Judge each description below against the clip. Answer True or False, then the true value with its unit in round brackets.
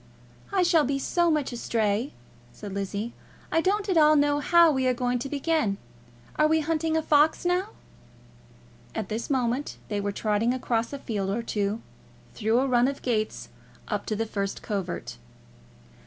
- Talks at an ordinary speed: True (170 wpm)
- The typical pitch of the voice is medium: False (255 Hz)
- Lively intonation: True (6.2 semitones)